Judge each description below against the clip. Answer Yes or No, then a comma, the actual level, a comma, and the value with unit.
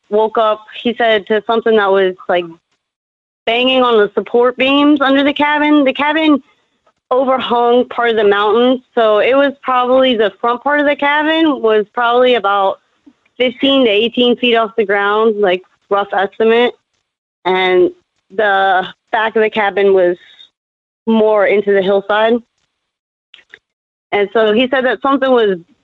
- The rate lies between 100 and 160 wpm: Yes, average, 150 wpm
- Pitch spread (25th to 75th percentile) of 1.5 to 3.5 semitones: No, average, 4.0 semitones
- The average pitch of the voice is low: No, high, 230 Hz